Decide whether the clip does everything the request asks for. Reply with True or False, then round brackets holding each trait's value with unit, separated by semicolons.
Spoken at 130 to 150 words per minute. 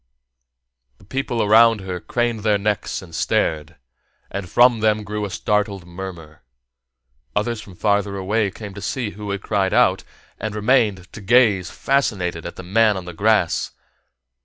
False (160 wpm)